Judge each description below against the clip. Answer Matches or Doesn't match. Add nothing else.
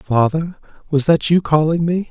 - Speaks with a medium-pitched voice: Matches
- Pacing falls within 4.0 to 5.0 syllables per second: Matches